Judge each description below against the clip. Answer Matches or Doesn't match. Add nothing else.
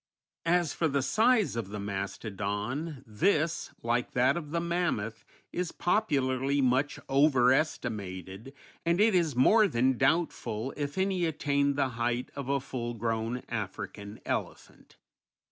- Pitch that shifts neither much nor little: Doesn't match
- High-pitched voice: Doesn't match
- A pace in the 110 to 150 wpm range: Matches